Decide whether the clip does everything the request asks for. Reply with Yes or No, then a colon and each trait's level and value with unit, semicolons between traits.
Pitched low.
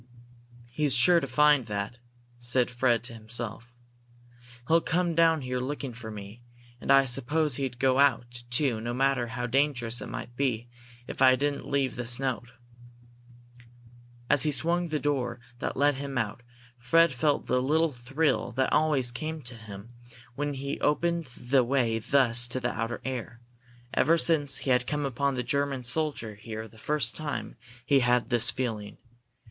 Yes: low, 130 Hz